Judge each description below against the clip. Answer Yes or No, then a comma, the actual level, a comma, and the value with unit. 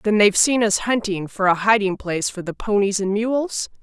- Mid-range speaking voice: No, high, 205 Hz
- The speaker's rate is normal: No, fast, 220 wpm